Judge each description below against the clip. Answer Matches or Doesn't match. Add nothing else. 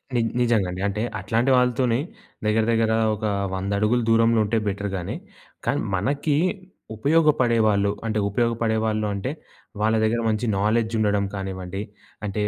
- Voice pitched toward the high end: Doesn't match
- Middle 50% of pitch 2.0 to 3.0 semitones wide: Matches